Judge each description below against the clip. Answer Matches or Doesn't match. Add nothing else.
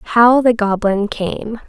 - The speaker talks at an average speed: Matches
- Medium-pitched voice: Doesn't match